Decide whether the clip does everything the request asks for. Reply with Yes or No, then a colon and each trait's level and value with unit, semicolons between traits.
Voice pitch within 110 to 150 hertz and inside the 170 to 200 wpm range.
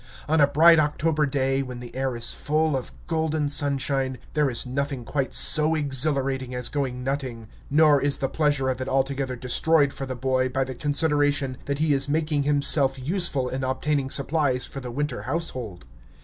Yes: medium, 140 Hz; average, 180 wpm